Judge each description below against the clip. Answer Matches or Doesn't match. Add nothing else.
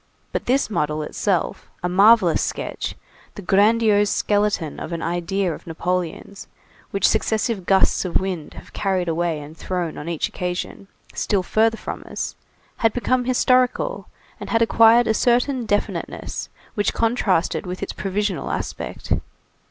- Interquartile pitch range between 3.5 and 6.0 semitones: Matches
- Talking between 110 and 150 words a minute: Matches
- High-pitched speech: Matches